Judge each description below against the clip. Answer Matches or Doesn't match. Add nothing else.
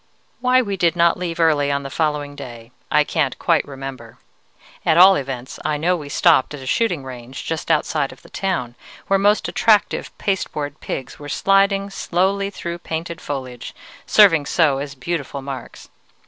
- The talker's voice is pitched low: Doesn't match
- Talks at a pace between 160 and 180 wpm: Matches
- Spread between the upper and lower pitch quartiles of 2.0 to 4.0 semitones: Doesn't match